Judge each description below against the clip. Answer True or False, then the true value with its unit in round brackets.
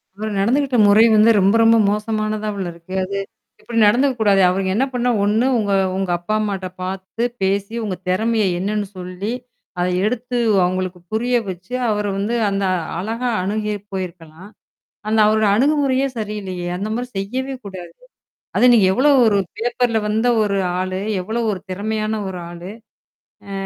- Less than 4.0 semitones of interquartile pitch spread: True (3.3 semitones)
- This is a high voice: True (210 Hz)